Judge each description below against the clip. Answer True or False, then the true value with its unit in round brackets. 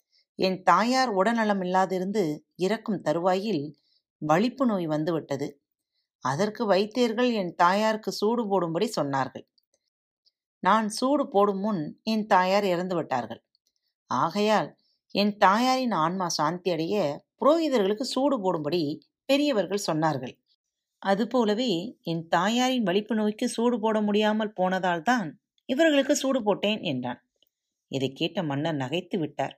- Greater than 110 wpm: False (105 wpm)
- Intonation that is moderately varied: True (5.0 semitones)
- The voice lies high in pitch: True (200 Hz)